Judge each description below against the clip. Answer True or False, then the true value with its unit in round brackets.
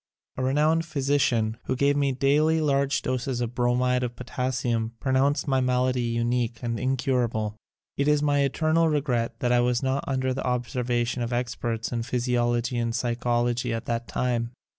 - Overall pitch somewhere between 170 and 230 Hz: False (125 Hz)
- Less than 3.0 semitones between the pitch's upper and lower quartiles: True (2.4 semitones)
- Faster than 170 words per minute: False (160 wpm)